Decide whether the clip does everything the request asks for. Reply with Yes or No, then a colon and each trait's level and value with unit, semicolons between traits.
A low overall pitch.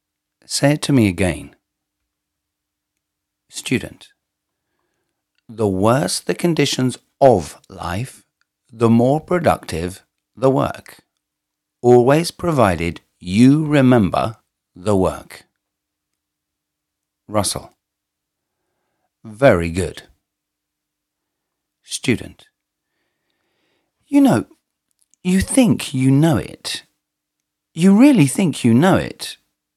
Yes: low, 120 Hz